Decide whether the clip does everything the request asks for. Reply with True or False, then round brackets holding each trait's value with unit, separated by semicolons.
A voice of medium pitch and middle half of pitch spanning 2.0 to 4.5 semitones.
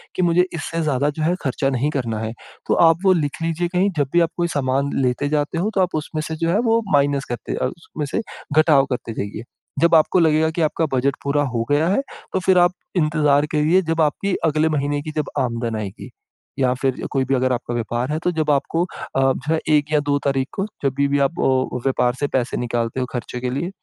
True (145 Hz; 3.9 semitones)